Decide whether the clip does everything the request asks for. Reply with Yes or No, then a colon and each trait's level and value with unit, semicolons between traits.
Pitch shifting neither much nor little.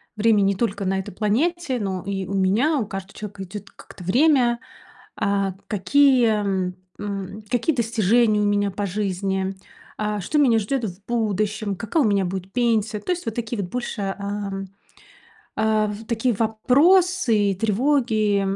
Yes: average, 3.3 semitones